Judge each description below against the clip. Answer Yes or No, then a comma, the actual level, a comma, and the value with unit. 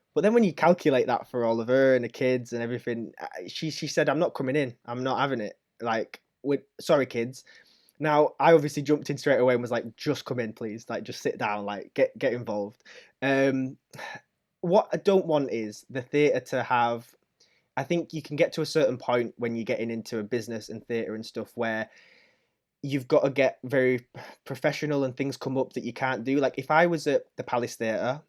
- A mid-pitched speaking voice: No, low, 130 Hz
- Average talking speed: No, fast, 220 wpm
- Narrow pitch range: No, average, 4.0 semitones